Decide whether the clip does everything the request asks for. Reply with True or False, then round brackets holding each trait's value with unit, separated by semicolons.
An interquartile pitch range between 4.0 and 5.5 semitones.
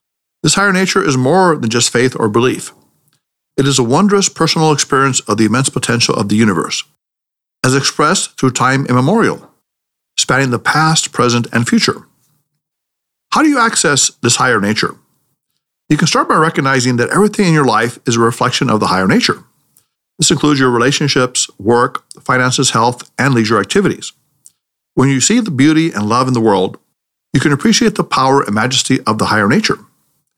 True (4.6 semitones)